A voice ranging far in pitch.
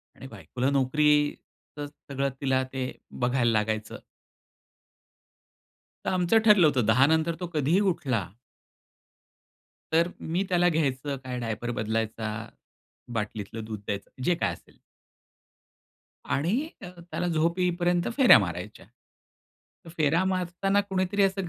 Yes: wide, 7.3 semitones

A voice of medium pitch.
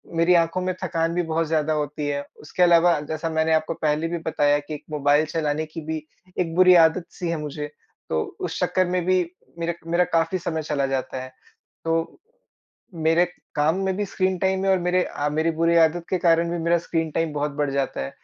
Yes: medium, 165 Hz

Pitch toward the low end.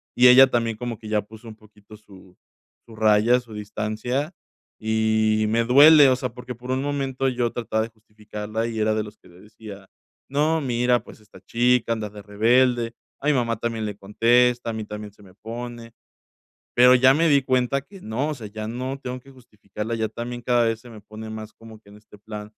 Yes: low, 115 Hz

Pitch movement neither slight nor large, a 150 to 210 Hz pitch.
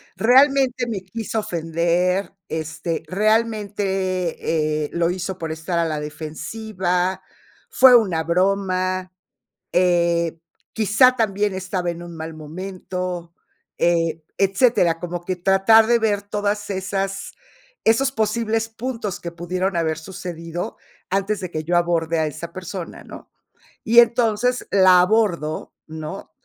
Yes: average, 3.8 semitones; medium, 185 Hz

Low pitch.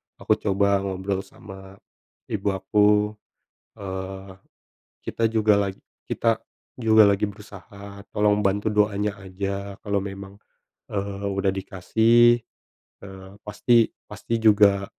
Yes: low, 100 Hz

